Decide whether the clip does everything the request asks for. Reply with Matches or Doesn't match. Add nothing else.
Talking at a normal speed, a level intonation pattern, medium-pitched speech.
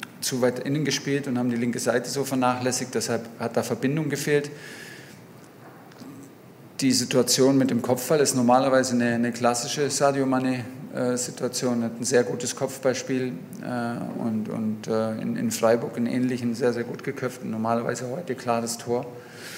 Doesn't match